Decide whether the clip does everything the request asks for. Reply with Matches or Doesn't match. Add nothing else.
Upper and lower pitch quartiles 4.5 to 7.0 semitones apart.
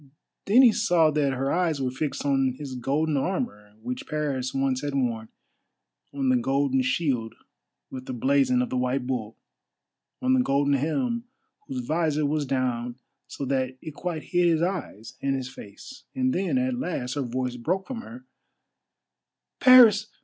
Matches